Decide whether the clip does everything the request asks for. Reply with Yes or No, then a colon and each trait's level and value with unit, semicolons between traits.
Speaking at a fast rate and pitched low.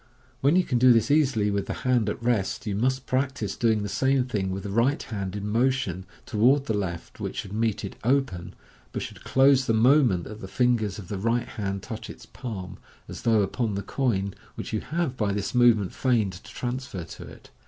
Yes: fast, 215 wpm; low, 110 Hz